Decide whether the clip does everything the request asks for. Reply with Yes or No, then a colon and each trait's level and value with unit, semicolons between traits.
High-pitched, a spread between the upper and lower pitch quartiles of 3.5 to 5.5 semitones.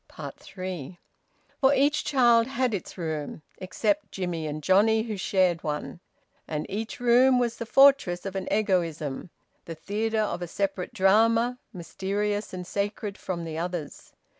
Yes: high, 195 Hz; average, 4.3 semitones